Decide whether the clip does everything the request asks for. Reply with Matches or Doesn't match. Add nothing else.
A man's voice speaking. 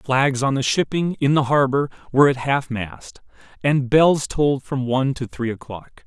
Matches